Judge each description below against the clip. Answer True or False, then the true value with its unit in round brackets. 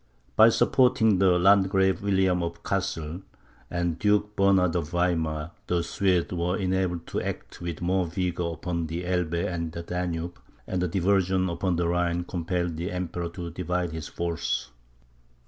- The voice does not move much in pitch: True (1.8 semitones)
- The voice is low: True (90 Hz)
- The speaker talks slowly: False (155 wpm)